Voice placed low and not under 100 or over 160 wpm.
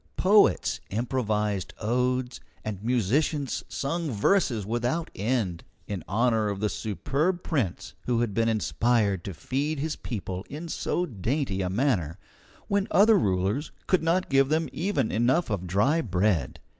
Yes: low, 120 Hz; average, 145 wpm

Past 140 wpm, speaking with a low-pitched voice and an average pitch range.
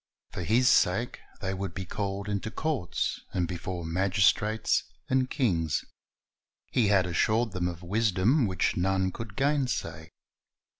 No: slow, 135 wpm; low, 100 Hz; average, 4.2 semitones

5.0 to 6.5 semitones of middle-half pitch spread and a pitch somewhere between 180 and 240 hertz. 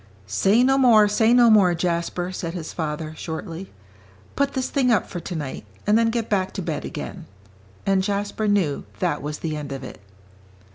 Yes: wide, 5.5 semitones; high, 190 Hz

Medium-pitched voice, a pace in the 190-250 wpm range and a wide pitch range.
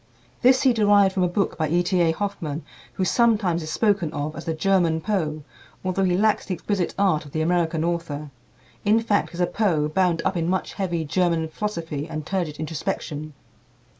No: medium, 175 Hz; average, 195 wpm; average, 3.7 semitones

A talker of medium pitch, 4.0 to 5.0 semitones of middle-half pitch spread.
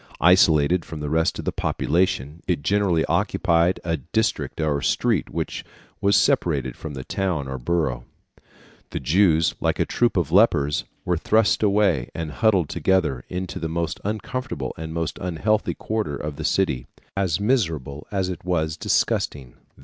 No: very low, 85 Hz; average, 4.4 semitones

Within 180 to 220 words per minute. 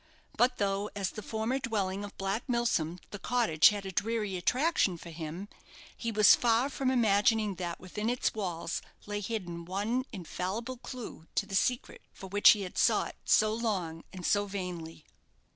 No: average, 170 wpm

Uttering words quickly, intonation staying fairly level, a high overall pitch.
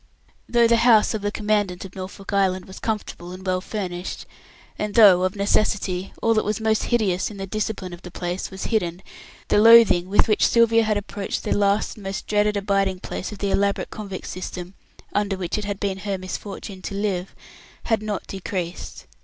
No: average, 195 wpm; narrow, 2.3 semitones; high, 200 Hz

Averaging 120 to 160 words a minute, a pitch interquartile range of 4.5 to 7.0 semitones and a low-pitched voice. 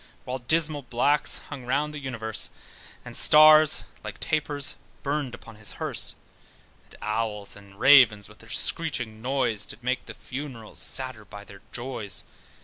Yes: average, 145 wpm; average, 4.8 semitones; low, 125 Hz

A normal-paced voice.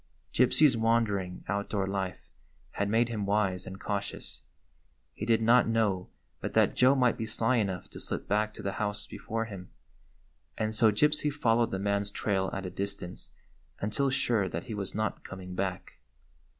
Yes: average, 170 wpm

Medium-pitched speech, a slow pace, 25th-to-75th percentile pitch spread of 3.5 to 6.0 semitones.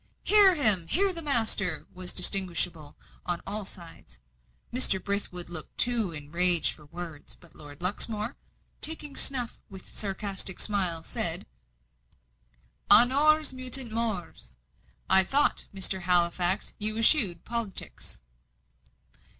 No: high, 195 Hz; slow, 115 wpm; average, 5.2 semitones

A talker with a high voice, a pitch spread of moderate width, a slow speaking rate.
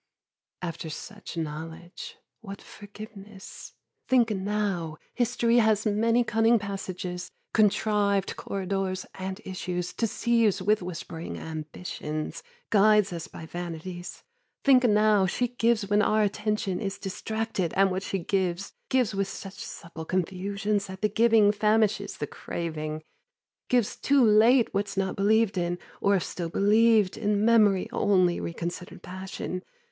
Yes: high, 200 Hz; average, 3.0 semitones; slow, 130 wpm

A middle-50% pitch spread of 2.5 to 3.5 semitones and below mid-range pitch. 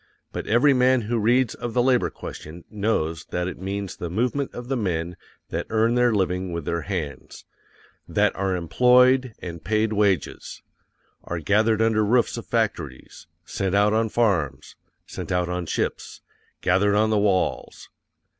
No: average, 4.7 semitones; low, 105 Hz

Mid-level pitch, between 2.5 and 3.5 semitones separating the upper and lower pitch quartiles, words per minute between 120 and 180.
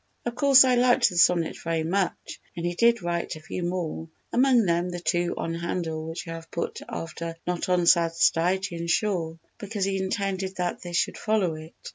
No: medium, 175 Hz; average, 2.8 semitones; average, 190 wpm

